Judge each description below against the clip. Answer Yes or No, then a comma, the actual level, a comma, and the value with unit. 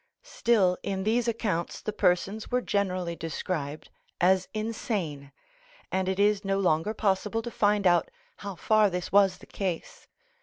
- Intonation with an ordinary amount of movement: Yes, average, 3.0 semitones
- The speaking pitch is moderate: No, high, 195 Hz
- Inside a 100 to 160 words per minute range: Yes, average, 150 wpm